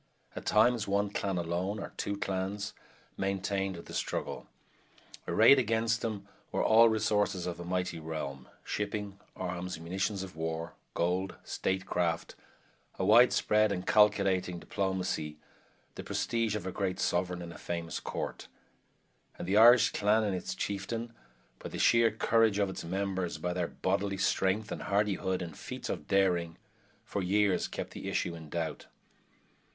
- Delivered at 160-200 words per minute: No, average, 150 wpm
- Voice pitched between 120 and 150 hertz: No, very low, 95 Hz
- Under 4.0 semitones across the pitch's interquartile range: Yes, average, 2.8 semitones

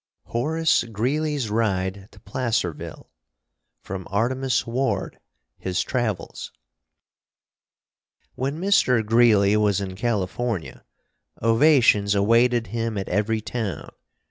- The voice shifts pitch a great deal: No, average, 3.8 semitones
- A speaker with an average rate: No, slow, 95 wpm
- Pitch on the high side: No, low, 115 Hz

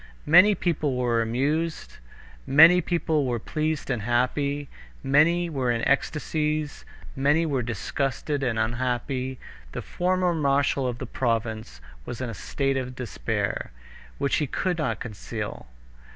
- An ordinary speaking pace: No, slow, 130 wpm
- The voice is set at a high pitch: No, low, 135 Hz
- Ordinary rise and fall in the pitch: Yes, average, 4.0 semitones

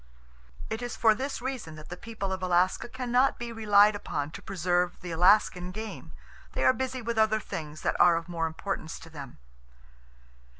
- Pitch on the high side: Yes, high, 195 Hz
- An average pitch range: Yes, average, 5.0 semitones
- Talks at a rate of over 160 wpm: Yes, average, 185 wpm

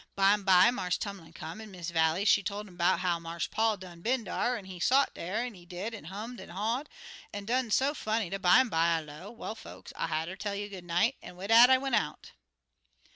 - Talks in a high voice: Yes, high, 200 Hz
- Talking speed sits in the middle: No, fast, 225 wpm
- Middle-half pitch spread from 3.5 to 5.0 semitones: Yes, average, 4.4 semitones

